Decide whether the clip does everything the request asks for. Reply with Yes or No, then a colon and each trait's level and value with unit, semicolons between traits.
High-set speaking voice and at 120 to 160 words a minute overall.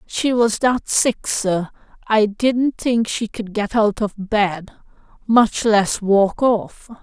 Yes: high, 215 Hz; average, 155 wpm